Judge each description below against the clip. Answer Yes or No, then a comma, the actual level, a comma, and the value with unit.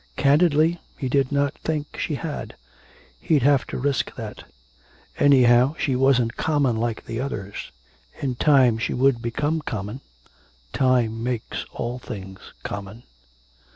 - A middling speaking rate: No, slow, 130 wpm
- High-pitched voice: No, low, 130 Hz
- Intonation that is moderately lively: Yes, average, 3.4 semitones